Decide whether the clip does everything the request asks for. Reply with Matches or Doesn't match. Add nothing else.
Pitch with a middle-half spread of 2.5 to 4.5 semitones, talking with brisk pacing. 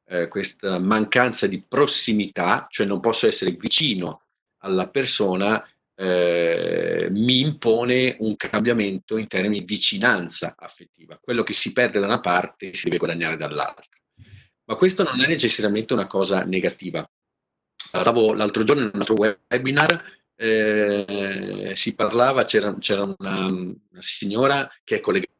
Doesn't match